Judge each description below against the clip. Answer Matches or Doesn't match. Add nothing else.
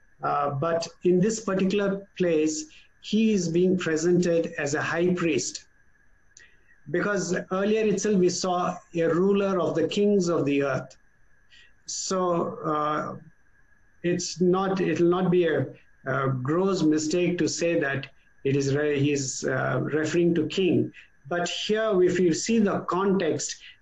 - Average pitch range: Matches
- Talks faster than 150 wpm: Doesn't match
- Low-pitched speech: Doesn't match